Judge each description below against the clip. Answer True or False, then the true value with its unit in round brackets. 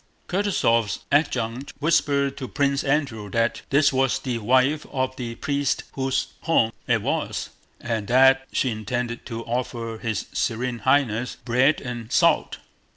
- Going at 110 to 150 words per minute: True (140 wpm)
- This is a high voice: False (125 Hz)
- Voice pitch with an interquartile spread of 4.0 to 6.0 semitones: False (3.2 semitones)